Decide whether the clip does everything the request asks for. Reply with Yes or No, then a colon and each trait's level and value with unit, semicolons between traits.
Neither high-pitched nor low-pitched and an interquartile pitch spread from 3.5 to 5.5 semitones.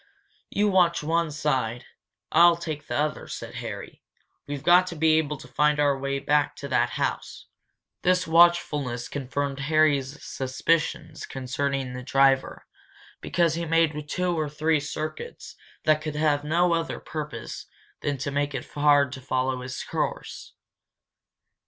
No: medium, 150 Hz; average, 2.9 semitones